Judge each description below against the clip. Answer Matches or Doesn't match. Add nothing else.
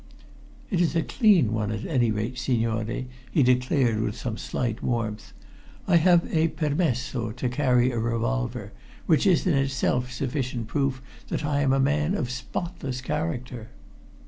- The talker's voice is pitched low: Matches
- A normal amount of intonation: Matches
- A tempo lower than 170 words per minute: Matches